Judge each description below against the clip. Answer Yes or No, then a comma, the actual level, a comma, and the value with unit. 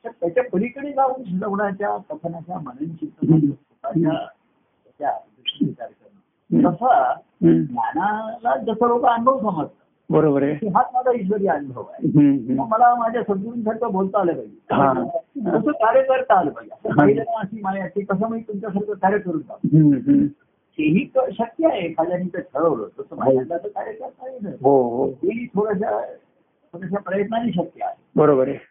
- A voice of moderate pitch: No, high, 210 Hz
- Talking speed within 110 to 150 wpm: Yes, average, 115 wpm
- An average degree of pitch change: No, wide, 6.2 semitones